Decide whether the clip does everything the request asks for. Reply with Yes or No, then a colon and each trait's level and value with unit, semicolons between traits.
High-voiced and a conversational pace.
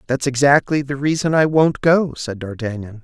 No: medium, 140 Hz; average, 180 wpm